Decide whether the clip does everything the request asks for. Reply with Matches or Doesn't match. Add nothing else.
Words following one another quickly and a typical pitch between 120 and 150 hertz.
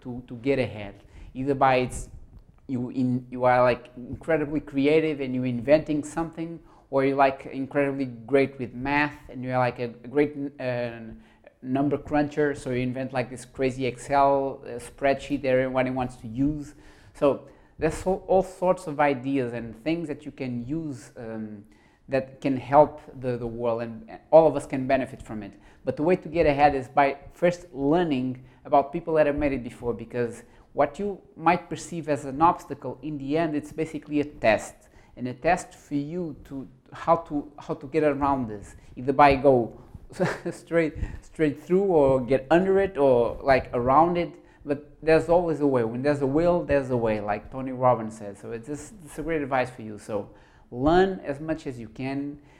Doesn't match